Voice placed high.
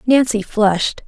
Yes: high, 220 Hz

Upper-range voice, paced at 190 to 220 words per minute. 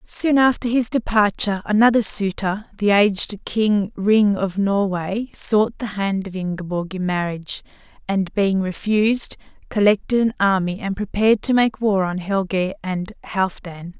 No: high, 200 Hz; average, 145 wpm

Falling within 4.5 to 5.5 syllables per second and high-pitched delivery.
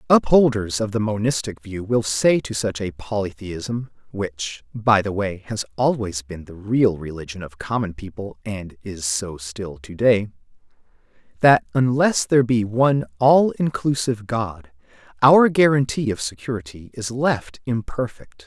No: 4.6 syllables/s; low, 110 Hz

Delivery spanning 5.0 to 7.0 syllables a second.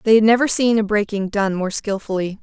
Yes: 5.7 syllables/s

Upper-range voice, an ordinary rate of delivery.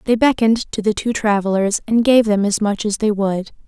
No: high, 215 Hz; fast, 230 wpm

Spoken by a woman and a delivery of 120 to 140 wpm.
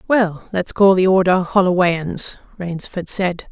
Yes: female; slow, 135 wpm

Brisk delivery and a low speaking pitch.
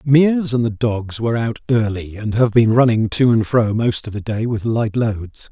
Yes: fast, 230 wpm; low, 115 Hz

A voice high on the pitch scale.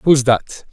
No: low, 130 Hz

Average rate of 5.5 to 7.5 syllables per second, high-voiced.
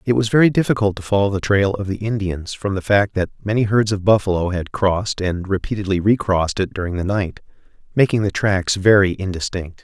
No: 5.7 syllables/s; low, 100 Hz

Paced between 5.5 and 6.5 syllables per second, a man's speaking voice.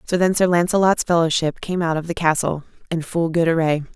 No: 5.9 syllables/s; female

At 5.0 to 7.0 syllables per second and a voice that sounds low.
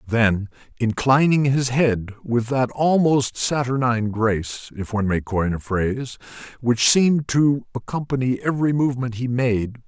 No: 4.8 syllables/s; low, 120 Hz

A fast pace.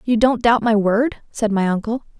Yes: fast, 220 wpm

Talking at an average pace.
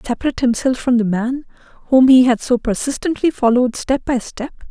Yes: average, 180 wpm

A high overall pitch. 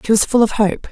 Yes: high, 215 Hz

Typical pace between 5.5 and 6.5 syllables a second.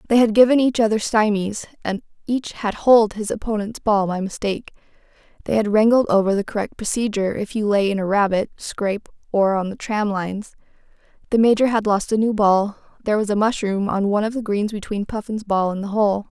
Yes: 5.9 syllables/s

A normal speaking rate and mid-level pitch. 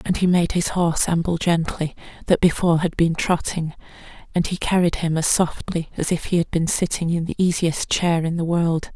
No: fast, 210 wpm; medium, 170 Hz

